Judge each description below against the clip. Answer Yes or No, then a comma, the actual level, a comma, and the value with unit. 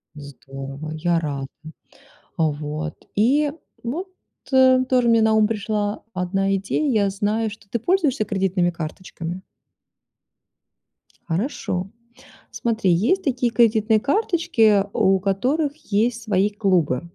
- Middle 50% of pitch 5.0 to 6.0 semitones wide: Yes, average, 5.3 semitones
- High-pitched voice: Yes, high, 205 Hz